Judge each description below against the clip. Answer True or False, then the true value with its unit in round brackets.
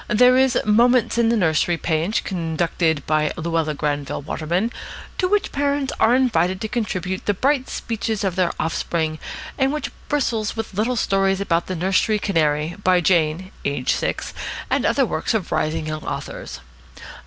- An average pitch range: False (6.2 semitones)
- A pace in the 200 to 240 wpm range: False (165 wpm)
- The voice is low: False (185 Hz)